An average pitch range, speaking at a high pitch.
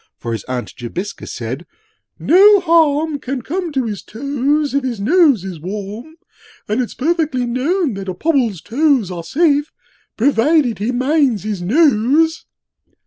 No: wide, 7.0 semitones; very high, 255 Hz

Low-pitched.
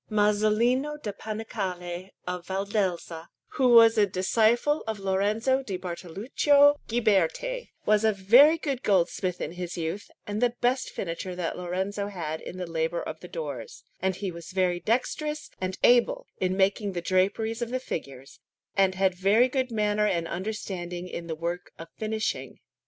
No: high, 195 Hz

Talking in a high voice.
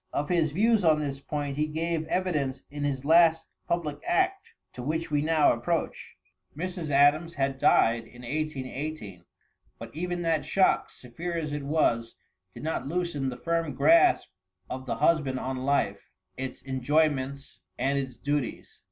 No: medium, 150 Hz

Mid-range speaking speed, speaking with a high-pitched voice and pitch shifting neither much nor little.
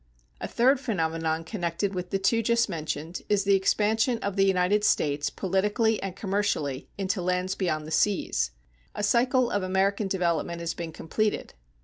Yes: average, 160 wpm; high, 195 Hz; average, 3.5 semitones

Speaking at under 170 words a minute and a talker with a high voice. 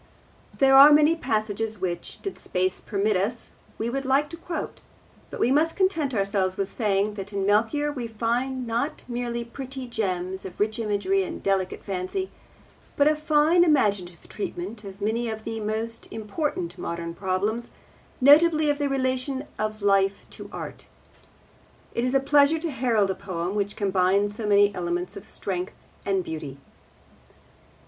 Yes: average, 160 wpm; high, 220 Hz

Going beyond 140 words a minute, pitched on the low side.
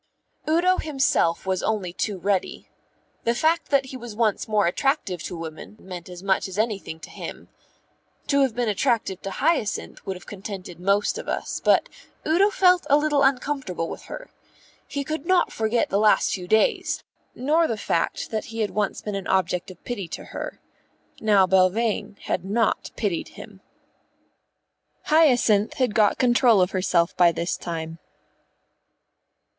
No: average, 160 wpm; high, 210 Hz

